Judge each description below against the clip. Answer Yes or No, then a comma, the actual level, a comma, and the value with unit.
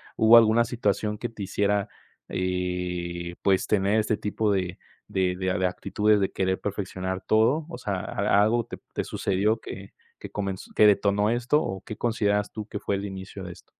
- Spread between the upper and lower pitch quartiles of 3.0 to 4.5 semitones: No, narrow, 2.4 semitones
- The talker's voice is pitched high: No, low, 100 Hz